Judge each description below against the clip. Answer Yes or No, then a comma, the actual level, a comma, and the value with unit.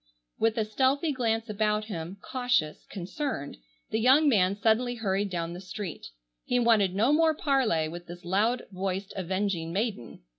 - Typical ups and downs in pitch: Yes, average, 4.9 semitones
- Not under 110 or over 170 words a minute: Yes, average, 155 wpm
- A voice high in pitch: Yes, high, 210 Hz